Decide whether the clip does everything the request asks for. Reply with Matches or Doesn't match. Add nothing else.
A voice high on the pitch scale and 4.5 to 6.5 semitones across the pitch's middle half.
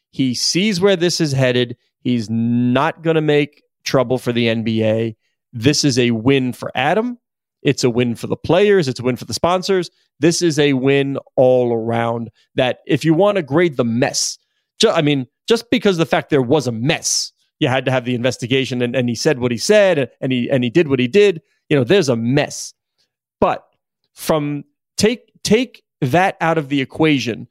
Doesn't match